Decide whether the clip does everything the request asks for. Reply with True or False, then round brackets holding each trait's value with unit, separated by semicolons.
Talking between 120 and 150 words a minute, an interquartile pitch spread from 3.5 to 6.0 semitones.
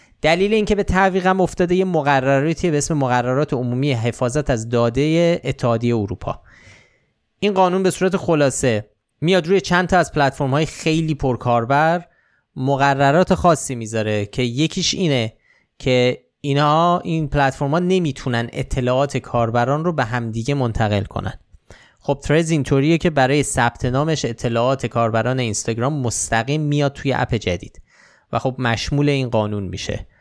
True (135 wpm; 5.1 semitones)